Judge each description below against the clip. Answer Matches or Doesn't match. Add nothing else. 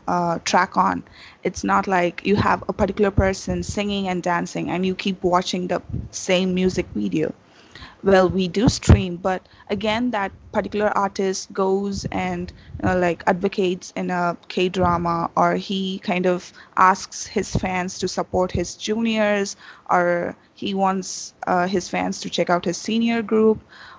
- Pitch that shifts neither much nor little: Doesn't match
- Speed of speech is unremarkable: Matches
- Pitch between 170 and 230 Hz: Matches